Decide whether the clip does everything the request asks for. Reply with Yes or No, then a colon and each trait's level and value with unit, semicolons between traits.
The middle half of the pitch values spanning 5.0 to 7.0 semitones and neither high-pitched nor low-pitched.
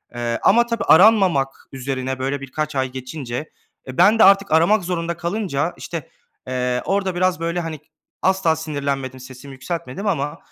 Yes: wide, 5.6 semitones; medium, 155 Hz